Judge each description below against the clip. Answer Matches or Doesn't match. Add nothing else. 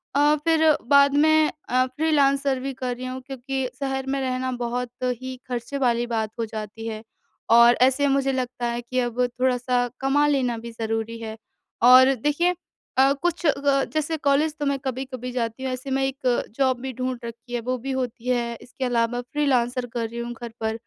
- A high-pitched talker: Matches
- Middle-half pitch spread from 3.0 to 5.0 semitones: Doesn't match